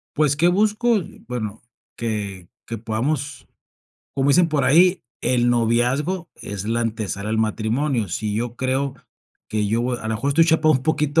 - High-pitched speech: No, low, 125 Hz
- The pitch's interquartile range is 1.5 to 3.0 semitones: No, wide, 5.4 semitones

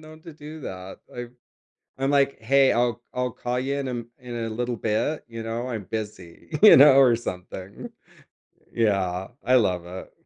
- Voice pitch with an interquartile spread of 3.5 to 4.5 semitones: Yes, average, 4.0 semitones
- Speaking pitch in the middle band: No, low, 120 Hz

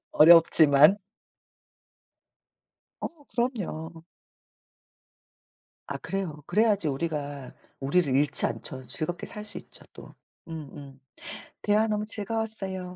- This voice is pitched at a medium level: Yes, medium, 170 Hz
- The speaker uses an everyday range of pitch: No, wide, 6.2 semitones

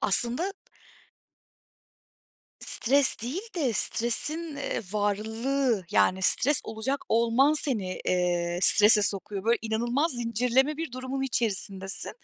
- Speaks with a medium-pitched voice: No, high, 235 Hz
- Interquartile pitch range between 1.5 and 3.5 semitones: No, average, 4.7 semitones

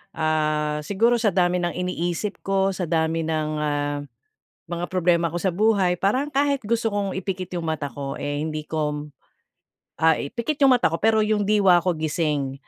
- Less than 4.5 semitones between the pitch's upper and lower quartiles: No, average, 4.8 semitones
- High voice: No, medium, 175 Hz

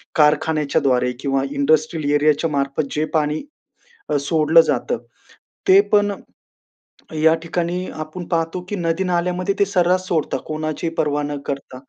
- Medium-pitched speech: Yes, medium, 155 Hz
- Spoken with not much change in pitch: No, average, 3.2 semitones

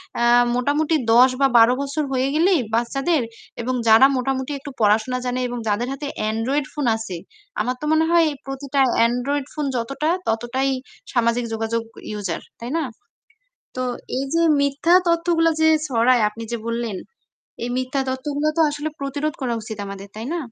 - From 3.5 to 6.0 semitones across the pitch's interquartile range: Yes, average, 3.8 semitones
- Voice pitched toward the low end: No, very high, 260 Hz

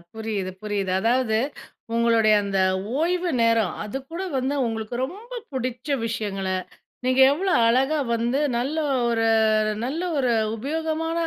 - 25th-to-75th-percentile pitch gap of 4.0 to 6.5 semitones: Yes, average, 5.2 semitones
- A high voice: Yes, high, 240 Hz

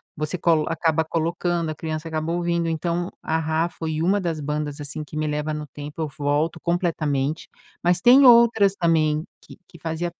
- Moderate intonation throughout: No, narrow, 2.0 semitones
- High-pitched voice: No, medium, 160 Hz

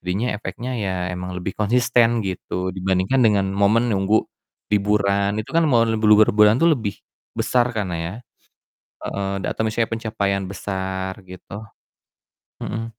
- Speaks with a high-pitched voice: No, low, 105 Hz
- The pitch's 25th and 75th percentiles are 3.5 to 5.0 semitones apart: No, average, 3.0 semitones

